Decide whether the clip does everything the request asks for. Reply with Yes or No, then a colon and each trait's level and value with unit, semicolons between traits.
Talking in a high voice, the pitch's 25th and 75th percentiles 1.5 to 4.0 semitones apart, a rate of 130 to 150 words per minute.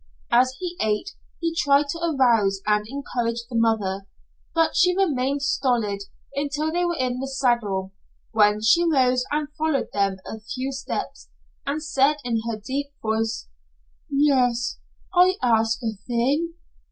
No: very high, 255 Hz; average, 4.8 semitones; average, 145 wpm